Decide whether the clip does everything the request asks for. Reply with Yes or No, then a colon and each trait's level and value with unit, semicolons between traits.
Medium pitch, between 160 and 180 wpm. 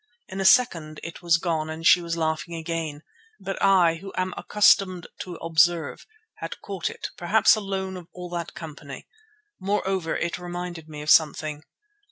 Yes: medium, 170 Hz; average, 165 wpm